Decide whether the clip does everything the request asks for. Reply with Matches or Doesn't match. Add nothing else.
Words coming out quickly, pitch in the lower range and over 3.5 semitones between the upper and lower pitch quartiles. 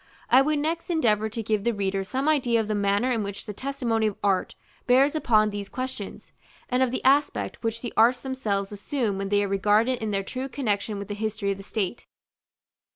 Doesn't match